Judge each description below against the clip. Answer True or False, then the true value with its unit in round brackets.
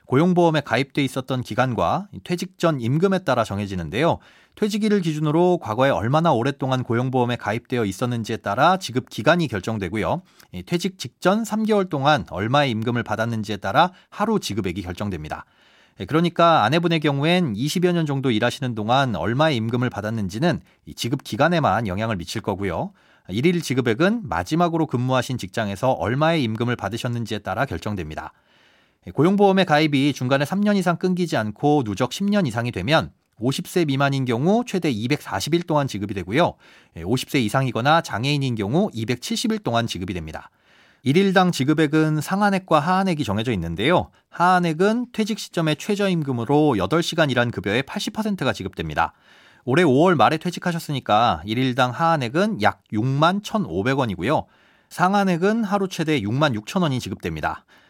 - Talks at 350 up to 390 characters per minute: True (355 characters per minute)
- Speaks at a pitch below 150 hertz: True (140 Hz)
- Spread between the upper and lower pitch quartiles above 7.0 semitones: True (7.5 semitones)